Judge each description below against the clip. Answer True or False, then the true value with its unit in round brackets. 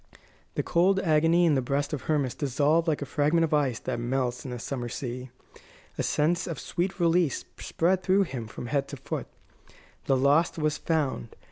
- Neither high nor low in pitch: True (150 Hz)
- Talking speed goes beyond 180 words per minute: True (190 wpm)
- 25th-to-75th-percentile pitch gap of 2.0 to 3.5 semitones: False (4.1 semitones)